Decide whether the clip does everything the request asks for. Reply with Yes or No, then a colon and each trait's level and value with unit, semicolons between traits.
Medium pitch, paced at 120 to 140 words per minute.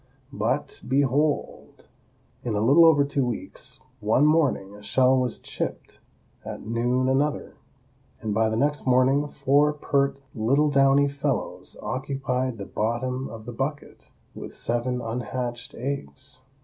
No: low, 130 Hz; slow, 135 wpm